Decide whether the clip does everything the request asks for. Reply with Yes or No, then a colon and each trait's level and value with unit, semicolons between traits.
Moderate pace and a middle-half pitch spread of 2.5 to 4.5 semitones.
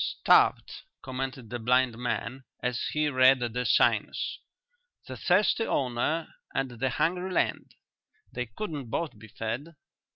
No: slow, 130 wpm; average, 3.8 semitones